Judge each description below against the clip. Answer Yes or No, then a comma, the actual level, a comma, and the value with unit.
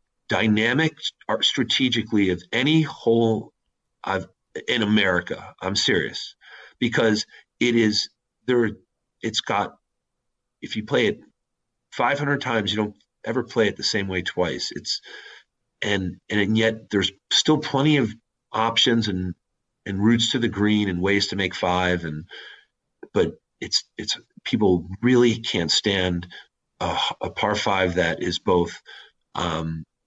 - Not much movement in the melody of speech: No, average, 3.9 semitones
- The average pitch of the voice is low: Yes, low, 110 Hz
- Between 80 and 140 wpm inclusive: Yes, slow, 135 wpm